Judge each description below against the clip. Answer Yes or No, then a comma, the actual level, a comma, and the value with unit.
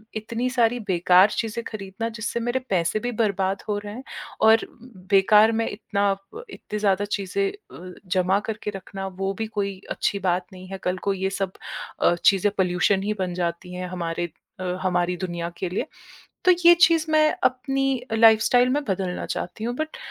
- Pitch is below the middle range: No, high, 200 Hz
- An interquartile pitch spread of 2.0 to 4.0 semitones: Yes, average, 3.7 semitones